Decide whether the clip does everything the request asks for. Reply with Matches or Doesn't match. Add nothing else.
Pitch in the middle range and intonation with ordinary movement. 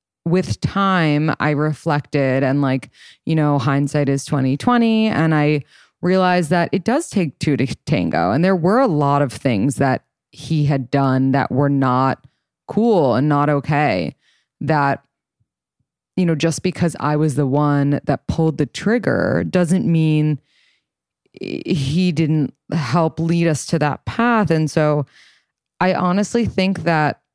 Matches